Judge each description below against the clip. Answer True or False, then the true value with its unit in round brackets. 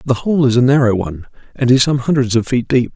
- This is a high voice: False (125 Hz)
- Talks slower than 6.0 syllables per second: False (6.4 syllables/s)